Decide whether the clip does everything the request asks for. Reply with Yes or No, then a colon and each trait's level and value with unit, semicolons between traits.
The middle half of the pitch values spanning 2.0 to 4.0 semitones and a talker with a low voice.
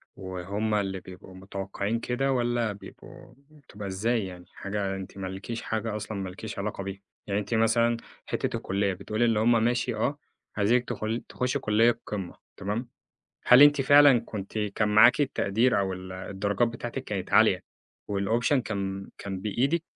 Yes: average, 3.4 semitones; low, 105 Hz